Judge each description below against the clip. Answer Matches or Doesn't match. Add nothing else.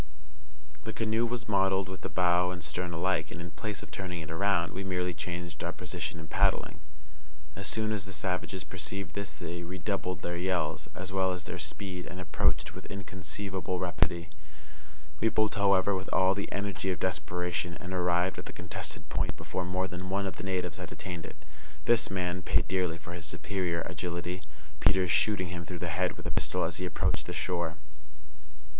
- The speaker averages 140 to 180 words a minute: Doesn't match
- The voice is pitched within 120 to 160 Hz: Doesn't match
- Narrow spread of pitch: Matches